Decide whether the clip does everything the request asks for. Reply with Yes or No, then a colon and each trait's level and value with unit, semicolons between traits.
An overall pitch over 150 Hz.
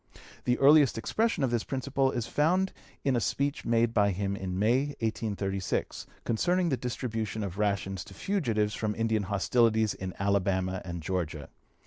No: low, 110 Hz